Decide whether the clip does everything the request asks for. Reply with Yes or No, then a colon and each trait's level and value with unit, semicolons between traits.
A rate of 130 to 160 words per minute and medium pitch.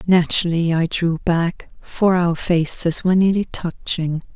Yes: average, 140 wpm; medium, 170 Hz